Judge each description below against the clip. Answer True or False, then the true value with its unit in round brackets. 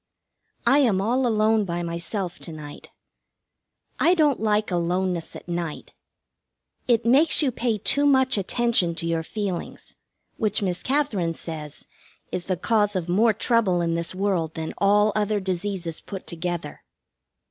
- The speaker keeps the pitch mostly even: False (4.6 semitones)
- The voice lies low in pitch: False (195 Hz)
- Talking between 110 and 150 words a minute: True (145 wpm)